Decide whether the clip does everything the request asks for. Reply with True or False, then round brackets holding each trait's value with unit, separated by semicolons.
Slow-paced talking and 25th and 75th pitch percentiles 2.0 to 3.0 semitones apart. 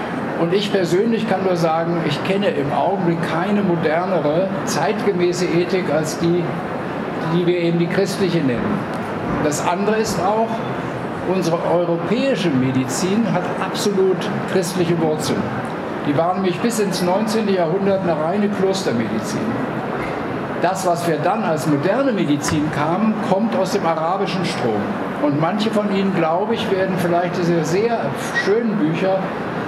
False (140 wpm; 2.7 semitones)